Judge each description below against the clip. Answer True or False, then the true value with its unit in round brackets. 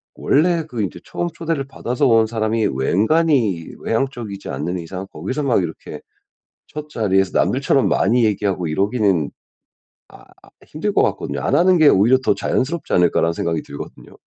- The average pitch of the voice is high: False (110 Hz)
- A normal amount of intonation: False (7.0 semitones)